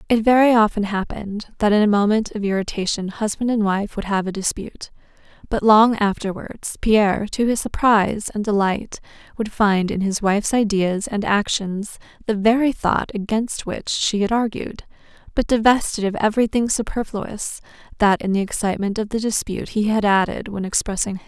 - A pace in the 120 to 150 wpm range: No, average, 170 wpm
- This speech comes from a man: No, female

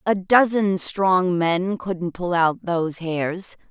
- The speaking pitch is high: No, medium, 180 Hz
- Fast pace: No, average, 145 wpm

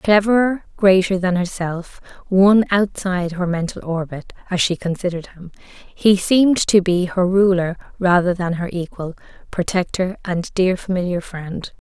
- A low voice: No, medium, 185 Hz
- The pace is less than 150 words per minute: Yes, average, 140 wpm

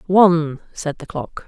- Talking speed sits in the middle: Yes, average, 160 wpm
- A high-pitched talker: No, medium, 165 Hz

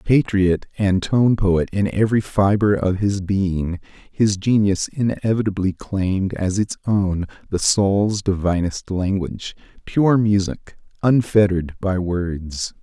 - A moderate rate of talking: No, slow, 120 wpm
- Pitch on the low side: Yes, low, 100 Hz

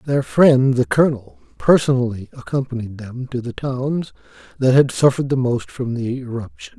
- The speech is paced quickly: No, average, 160 wpm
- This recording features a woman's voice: No, male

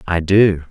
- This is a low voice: Yes, very low, 90 Hz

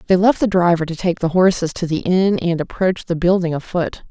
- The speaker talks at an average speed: No, fast, 235 wpm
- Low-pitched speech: No, medium, 175 Hz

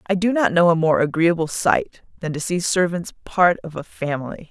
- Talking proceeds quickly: Yes, fast, 215 wpm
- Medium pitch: Yes, medium, 170 Hz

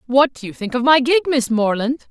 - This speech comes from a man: No, female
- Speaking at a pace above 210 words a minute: Yes, fast, 255 wpm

